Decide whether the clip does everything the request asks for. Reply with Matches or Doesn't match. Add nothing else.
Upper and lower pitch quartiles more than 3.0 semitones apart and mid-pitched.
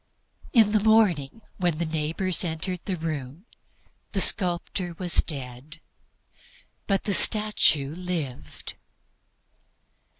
Matches